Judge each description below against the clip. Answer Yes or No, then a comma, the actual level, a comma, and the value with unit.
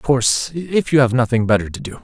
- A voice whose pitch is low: Yes, low, 125 Hz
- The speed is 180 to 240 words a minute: No, fast, 265 wpm